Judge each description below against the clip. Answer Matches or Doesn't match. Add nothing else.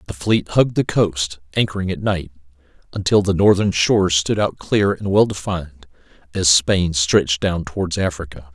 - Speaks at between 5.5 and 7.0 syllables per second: Doesn't match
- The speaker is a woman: Doesn't match